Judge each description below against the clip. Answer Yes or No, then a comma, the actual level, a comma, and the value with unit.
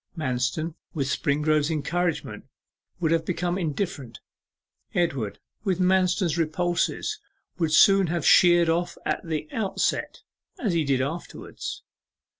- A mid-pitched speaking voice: Yes, medium, 165 Hz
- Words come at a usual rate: No, slow, 110 wpm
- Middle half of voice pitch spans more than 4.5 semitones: No, average, 2.9 semitones